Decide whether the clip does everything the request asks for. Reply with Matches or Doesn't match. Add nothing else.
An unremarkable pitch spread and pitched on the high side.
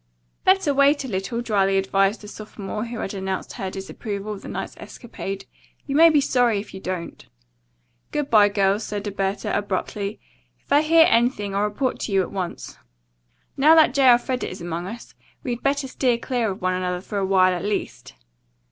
Matches